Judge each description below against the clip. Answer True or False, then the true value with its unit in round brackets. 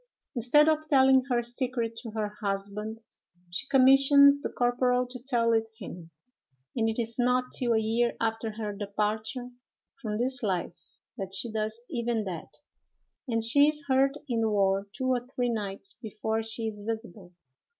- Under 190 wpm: True (165 wpm)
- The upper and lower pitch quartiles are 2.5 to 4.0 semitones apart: True (2.9 semitones)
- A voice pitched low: False (230 Hz)